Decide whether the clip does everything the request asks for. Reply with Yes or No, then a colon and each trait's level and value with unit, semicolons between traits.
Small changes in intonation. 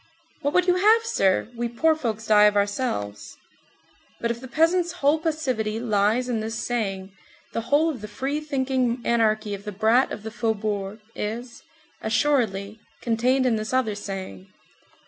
No: average, 4.2 semitones